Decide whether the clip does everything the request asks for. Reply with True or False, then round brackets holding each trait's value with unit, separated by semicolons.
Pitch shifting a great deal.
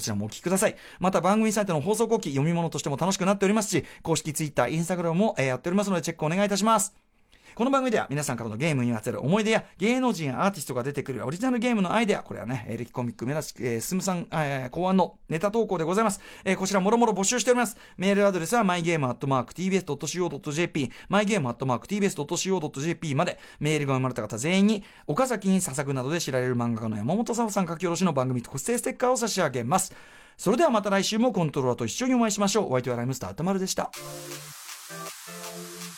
True (7.2 semitones)